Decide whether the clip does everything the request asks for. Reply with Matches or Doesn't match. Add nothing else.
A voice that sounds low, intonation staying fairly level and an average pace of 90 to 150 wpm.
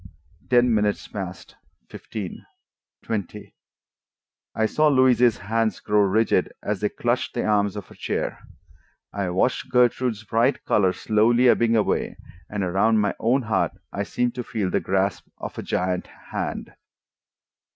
Doesn't match